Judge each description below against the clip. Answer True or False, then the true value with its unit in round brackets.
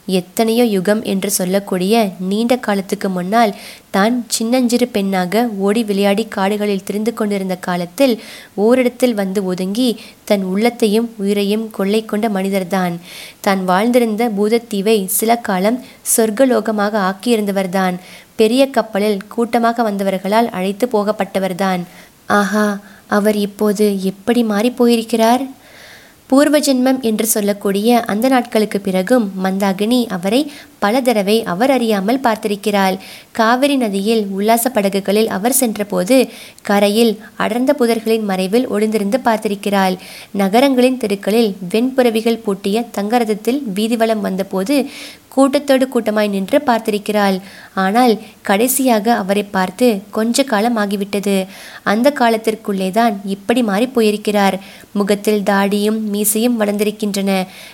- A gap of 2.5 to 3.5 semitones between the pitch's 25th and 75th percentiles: True (2.9 semitones)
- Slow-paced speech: False (100 wpm)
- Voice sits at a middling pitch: False (215 Hz)